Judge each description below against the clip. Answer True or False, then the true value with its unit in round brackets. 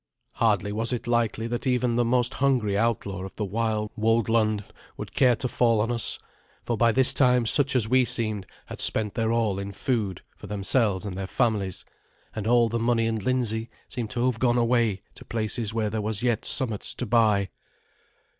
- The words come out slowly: False (190 wpm)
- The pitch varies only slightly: True (2.3 semitones)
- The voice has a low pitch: True (115 Hz)